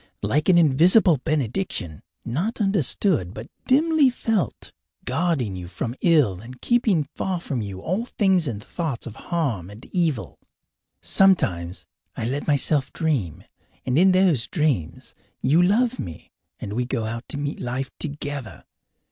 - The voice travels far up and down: Yes, wide, 7.7 semitones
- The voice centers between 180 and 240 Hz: No, medium, 145 Hz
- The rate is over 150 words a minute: No, average, 145 wpm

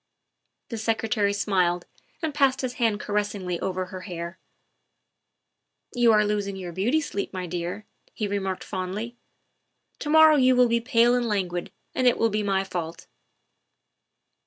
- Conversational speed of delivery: Yes, average, 160 wpm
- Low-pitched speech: No, high, 205 Hz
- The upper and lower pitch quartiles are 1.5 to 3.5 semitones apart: No, average, 4.3 semitones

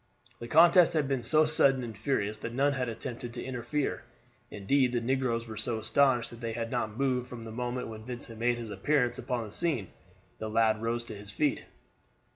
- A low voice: Yes, low, 120 Hz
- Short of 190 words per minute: No, fast, 205 wpm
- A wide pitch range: No, average, 2.8 semitones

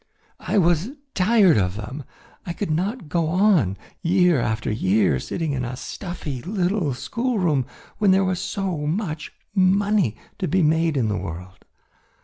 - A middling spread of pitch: No, wide, 7.0 semitones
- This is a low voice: No, medium, 170 Hz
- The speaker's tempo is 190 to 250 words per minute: No, average, 150 wpm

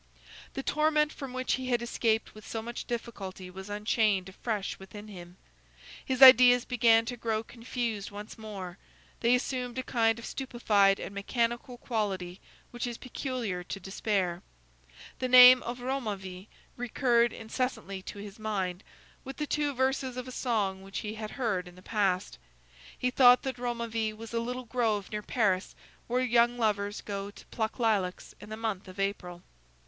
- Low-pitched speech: No, high, 225 Hz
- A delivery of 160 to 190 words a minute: Yes, average, 165 wpm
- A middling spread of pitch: Yes, average, 3.7 semitones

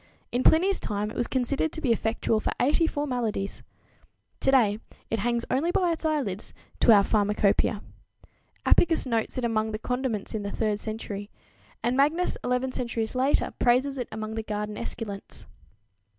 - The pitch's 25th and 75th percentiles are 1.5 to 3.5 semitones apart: No, average, 3.9 semitones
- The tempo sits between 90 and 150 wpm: No, average, 160 wpm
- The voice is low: No, high, 235 Hz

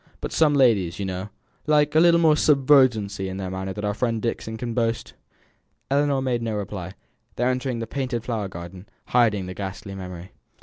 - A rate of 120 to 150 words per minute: No, average, 185 wpm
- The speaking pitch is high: No, low, 115 Hz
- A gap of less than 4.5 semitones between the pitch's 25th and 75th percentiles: No, wide, 5.4 semitones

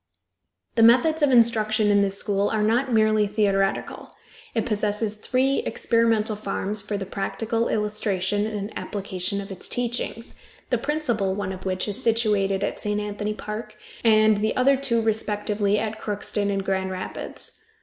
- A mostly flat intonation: Yes, narrow, 2.1 semitones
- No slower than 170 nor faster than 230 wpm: No, average, 155 wpm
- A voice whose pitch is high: Yes, high, 210 Hz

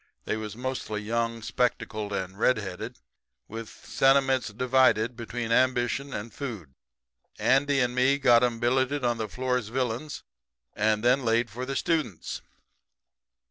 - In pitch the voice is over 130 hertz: No, low, 120 Hz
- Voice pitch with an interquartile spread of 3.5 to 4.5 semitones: No, average, 3.0 semitones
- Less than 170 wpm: Yes, slow, 135 wpm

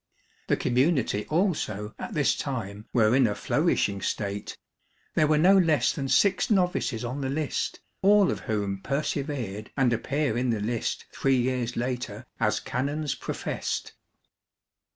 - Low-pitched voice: Yes, low, 130 Hz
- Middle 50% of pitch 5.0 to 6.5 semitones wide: Yes, wide, 5.5 semitones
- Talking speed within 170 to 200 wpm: No, average, 145 wpm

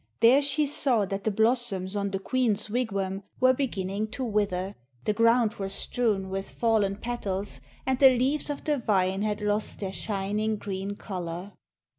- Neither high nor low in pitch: No, high, 210 Hz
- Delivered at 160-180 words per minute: Yes, average, 165 wpm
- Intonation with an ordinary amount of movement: Yes, average, 3.8 semitones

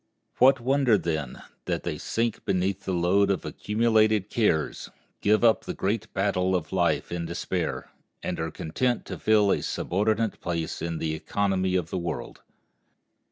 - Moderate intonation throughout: Yes, average, 4.1 semitones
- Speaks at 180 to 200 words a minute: No, average, 160 wpm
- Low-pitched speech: Yes, very low, 95 Hz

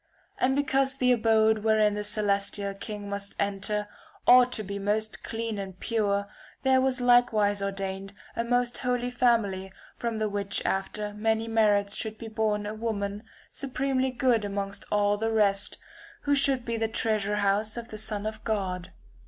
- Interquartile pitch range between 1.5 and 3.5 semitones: Yes, narrow, 2.6 semitones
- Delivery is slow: No, average, 170 wpm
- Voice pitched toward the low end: No, high, 215 Hz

